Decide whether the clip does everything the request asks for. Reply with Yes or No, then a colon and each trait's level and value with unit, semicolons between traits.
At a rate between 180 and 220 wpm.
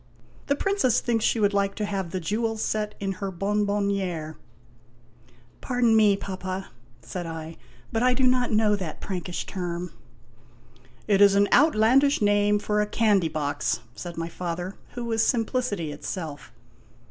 No: average, 155 wpm